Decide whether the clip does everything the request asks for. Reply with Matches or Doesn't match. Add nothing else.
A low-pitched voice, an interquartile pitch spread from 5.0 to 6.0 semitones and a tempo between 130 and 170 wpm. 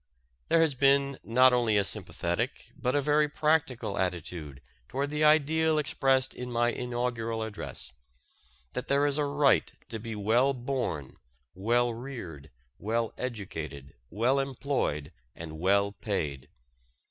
Matches